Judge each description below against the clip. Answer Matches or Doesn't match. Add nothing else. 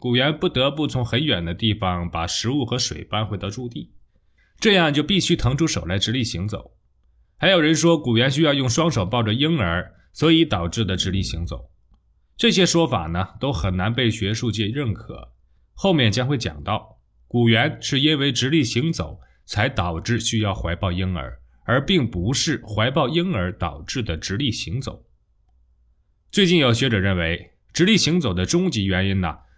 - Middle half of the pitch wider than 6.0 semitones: Matches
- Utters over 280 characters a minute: Doesn't match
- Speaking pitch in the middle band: Doesn't match